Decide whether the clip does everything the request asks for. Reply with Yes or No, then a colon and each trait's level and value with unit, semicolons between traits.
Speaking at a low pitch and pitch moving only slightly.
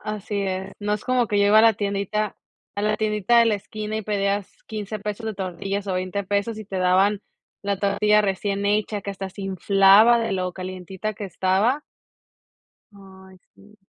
No: high, 200 Hz; narrow, 1.7 semitones